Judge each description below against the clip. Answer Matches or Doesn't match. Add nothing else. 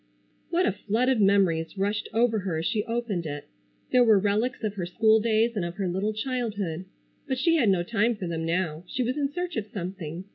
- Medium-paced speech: Doesn't match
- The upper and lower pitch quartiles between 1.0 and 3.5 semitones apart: Doesn't match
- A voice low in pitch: Doesn't match